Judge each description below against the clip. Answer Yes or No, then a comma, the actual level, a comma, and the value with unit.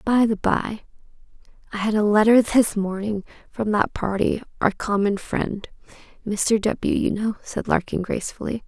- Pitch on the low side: No, high, 210 Hz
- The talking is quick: No, average, 145 wpm